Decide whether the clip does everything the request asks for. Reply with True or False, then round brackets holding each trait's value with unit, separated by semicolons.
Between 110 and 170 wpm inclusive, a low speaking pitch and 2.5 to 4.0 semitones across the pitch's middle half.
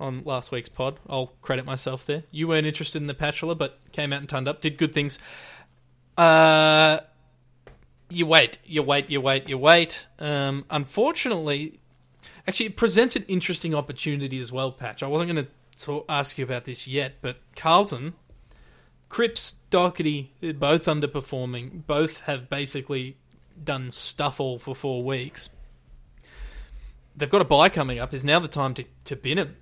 False (165 wpm; 145 Hz; 3.4 semitones)